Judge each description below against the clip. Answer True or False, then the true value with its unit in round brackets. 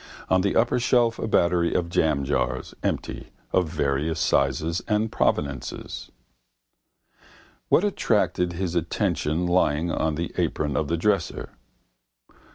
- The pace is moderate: False (120 wpm)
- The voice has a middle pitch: False (85 Hz)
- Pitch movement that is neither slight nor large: True (4.1 semitones)